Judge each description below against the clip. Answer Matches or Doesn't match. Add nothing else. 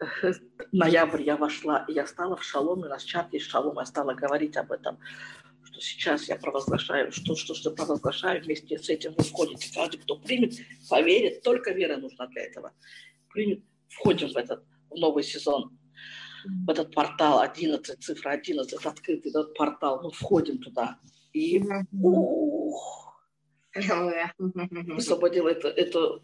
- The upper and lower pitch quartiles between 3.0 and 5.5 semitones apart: Matches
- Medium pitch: Matches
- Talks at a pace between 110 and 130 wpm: Doesn't match